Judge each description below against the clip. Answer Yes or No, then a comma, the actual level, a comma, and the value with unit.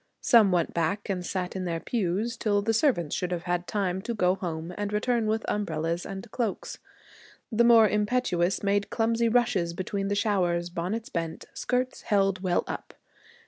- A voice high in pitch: Yes, high, 195 Hz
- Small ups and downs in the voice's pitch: No, average, 4.0 semitones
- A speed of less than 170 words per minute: No, average, 175 wpm